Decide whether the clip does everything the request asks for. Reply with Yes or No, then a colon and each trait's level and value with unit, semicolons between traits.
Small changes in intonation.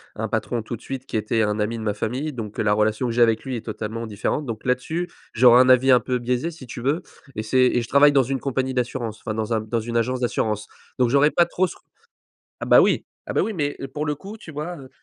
No: average, 3.7 semitones